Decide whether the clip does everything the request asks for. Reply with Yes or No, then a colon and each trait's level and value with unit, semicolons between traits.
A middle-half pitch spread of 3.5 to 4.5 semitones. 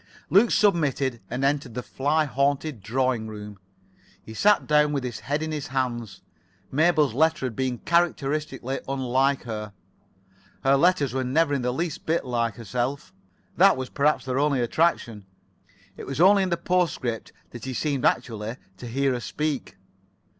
Yes: average, 3.9 semitones